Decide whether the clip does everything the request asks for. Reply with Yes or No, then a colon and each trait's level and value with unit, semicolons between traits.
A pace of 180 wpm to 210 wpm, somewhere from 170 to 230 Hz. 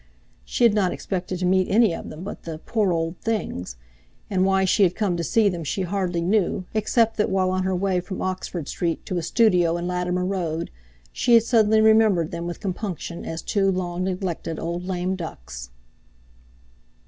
Yes: average, 190 wpm; medium, 185 Hz